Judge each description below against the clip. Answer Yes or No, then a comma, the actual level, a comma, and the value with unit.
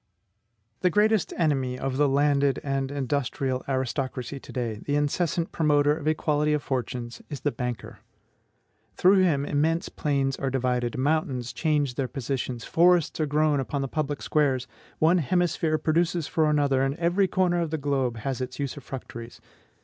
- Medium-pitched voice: Yes, medium, 145 Hz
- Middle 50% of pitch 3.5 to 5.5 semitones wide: No, average, 3.0 semitones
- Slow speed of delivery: No, average, 155 wpm